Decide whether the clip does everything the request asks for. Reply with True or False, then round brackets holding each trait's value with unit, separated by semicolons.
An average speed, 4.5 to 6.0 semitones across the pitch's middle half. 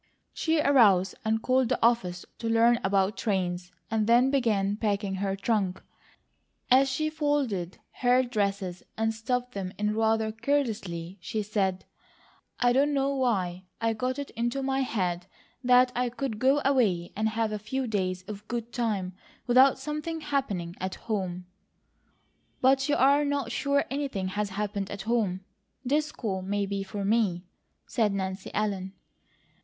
True (155 wpm; 4.8 semitones)